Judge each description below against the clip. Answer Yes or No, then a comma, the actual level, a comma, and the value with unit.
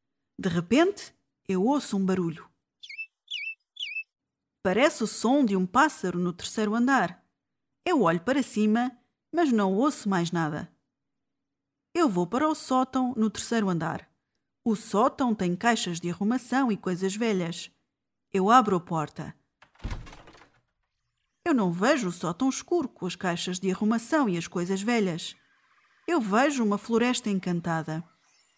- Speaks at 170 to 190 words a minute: No, average, 135 wpm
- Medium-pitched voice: No, high, 210 Hz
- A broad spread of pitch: Yes, wide, 6.4 semitones